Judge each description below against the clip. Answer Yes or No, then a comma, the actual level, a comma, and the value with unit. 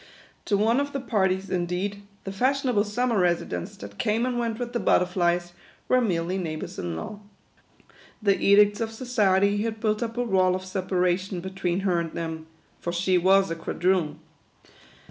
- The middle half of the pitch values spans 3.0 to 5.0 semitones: Yes, average, 3.8 semitones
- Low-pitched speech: No, high, 190 Hz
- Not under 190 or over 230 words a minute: No, average, 170 wpm